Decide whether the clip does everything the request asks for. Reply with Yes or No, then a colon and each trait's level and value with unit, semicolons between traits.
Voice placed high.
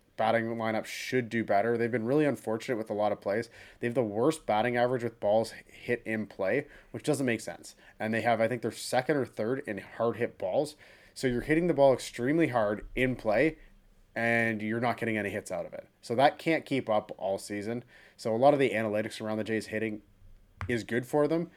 No: low, 115 Hz